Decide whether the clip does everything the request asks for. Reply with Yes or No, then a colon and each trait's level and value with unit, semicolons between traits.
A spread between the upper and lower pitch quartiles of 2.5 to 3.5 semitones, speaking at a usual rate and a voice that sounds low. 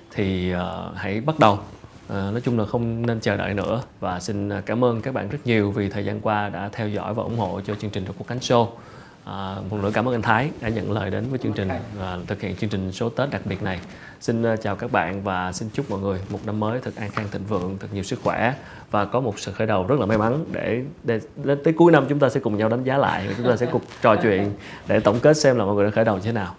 No: average, 2.9 semitones; fast, 285 wpm; low, 105 Hz